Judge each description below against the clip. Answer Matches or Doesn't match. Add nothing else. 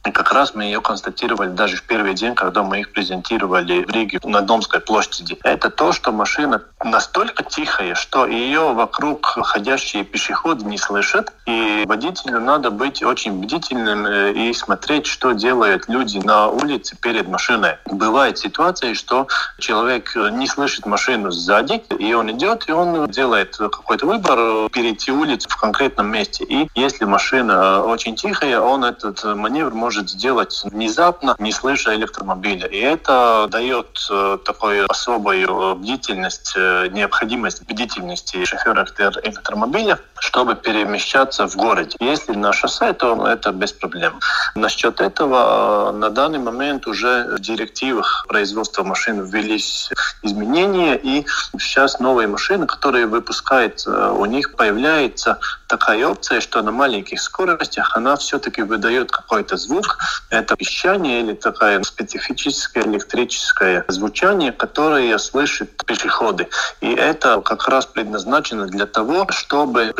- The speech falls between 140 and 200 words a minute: Doesn't match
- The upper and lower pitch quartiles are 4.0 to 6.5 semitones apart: Matches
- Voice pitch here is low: Matches